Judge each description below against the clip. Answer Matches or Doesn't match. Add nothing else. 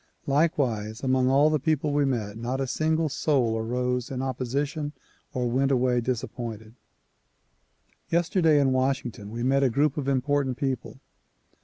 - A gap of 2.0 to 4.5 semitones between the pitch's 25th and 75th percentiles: Matches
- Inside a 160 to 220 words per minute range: Doesn't match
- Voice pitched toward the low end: Matches